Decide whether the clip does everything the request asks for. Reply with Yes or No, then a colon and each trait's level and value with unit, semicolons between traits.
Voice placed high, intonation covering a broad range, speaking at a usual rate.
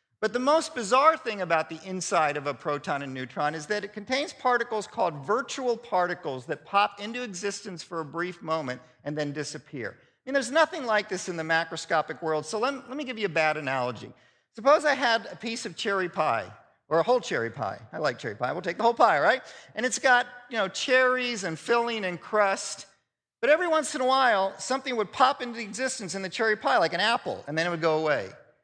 No: high, 200 Hz; wide, 7.3 semitones; fast, 230 wpm